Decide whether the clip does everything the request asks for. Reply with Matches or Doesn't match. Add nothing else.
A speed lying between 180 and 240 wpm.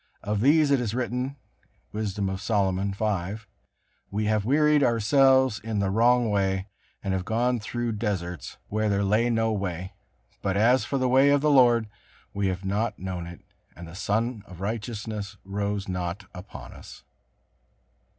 Doesn't match